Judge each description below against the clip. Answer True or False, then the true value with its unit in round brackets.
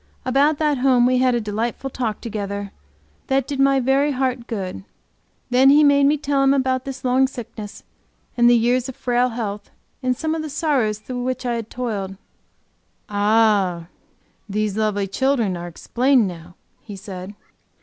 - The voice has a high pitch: True (245 Hz)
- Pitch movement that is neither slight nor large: True (4.3 semitones)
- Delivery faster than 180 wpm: False (170 wpm)